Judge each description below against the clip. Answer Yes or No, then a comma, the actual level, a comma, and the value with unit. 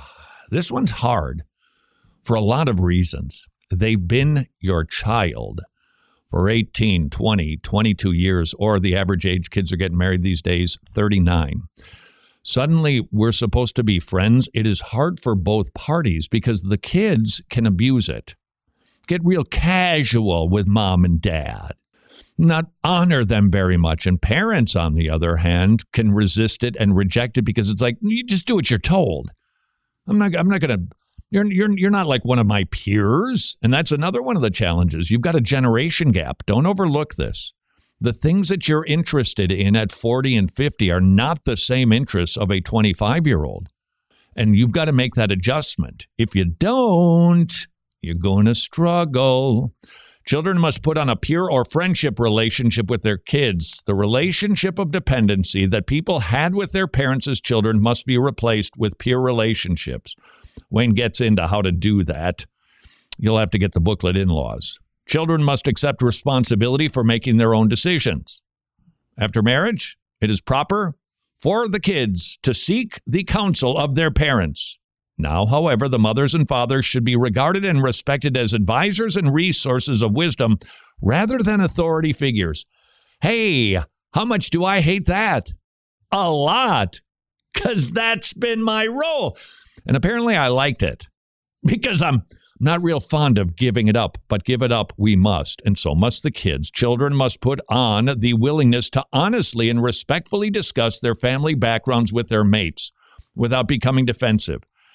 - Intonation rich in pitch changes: Yes, wide, 7.0 semitones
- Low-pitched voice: Yes, low, 120 Hz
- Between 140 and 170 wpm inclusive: Yes, average, 165 wpm